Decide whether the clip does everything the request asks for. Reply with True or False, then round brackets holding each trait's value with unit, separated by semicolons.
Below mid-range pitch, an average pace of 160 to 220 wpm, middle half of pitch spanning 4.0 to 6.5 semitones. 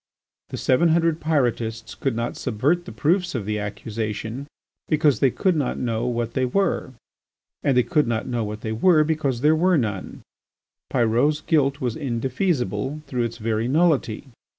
True (130 Hz; 165 wpm; 5.1 semitones)